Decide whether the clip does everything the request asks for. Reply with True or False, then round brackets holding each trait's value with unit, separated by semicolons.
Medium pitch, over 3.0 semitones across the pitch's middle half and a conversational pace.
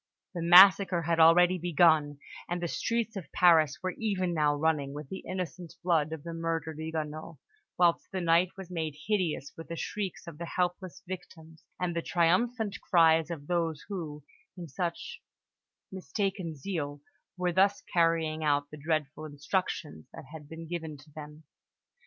False (165 Hz; 2.7 semitones; 160 wpm)